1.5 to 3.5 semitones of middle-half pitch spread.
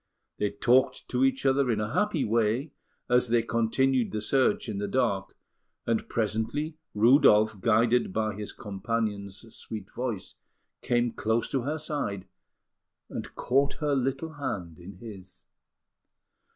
No: average, 3.9 semitones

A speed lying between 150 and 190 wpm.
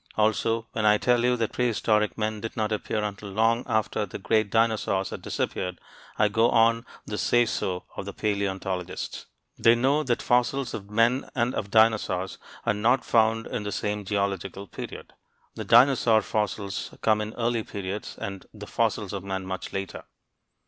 Yes: average, 170 wpm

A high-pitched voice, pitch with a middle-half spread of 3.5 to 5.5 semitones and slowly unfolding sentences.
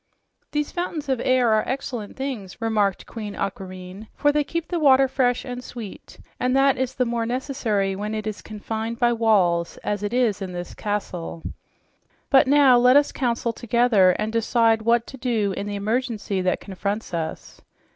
No: high, 230 Hz; average, 3.9 semitones; average, 175 wpm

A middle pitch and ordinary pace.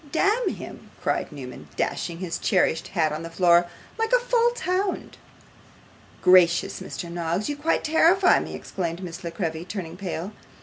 Yes: medium, 180 Hz; average, 160 wpm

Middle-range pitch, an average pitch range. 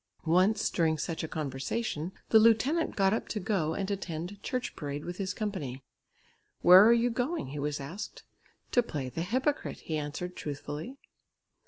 No: medium, 180 Hz; wide, 6.4 semitones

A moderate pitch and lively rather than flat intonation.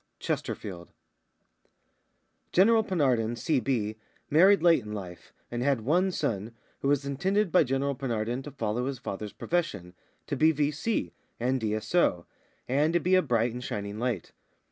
No: low, 130 Hz; wide, 6.6 semitones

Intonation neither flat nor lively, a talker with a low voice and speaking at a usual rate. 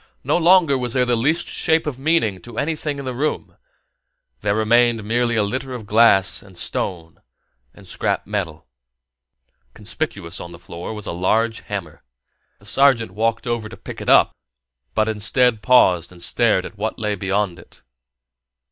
Yes: average, 4.4 semitones; low, 110 Hz; average, 165 wpm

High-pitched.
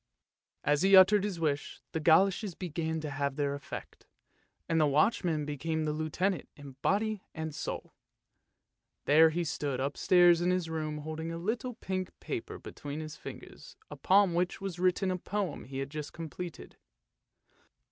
No: medium, 165 Hz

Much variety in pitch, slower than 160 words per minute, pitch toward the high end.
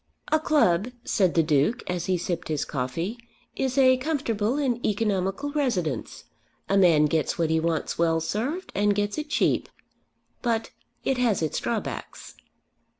Yes: wide, 7.4 semitones; average, 150 wpm; high, 205 Hz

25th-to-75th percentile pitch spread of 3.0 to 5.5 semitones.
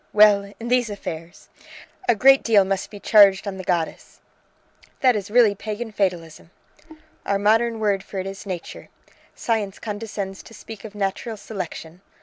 No: narrow, 2.4 semitones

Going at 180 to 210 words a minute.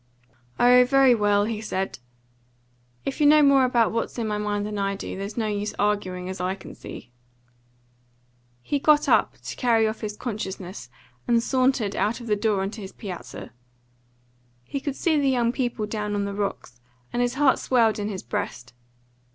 Yes: average, 185 wpm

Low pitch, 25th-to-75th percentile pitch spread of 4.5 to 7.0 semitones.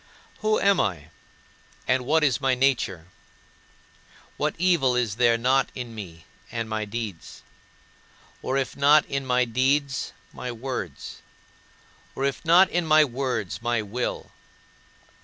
No: low, 125 Hz; average, 3.5 semitones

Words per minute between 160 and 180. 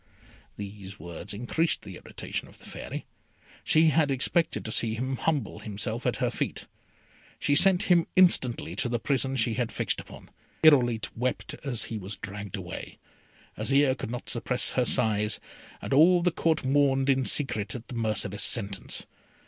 Yes: average, 165 wpm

